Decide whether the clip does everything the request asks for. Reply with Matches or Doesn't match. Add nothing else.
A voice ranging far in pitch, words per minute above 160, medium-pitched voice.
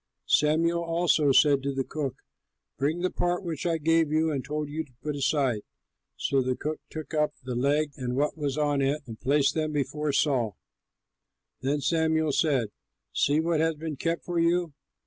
Doesn't match